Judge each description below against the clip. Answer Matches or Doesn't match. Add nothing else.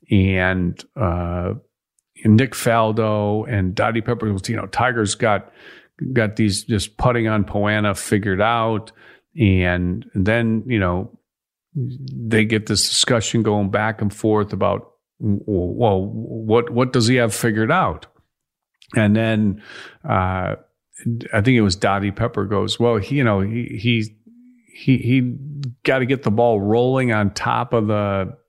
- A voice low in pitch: Matches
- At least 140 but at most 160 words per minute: Matches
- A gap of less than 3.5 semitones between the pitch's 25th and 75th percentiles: Matches